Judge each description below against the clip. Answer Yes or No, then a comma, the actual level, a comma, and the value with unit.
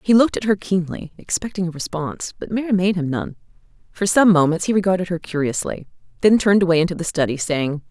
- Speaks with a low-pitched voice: No, medium, 180 Hz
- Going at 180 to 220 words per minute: Yes, fast, 205 wpm